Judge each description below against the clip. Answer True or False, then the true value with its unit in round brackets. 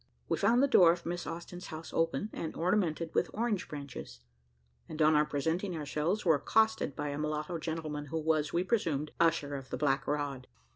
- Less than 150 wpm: False (190 wpm)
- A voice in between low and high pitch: True (160 Hz)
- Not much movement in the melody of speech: False (3.0 semitones)